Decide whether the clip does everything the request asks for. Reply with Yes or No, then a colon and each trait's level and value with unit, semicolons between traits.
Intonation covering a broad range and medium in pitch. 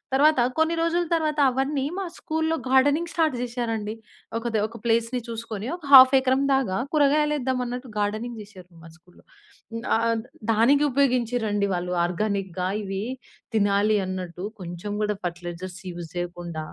No: wide, 5.9 semitones; high, 230 Hz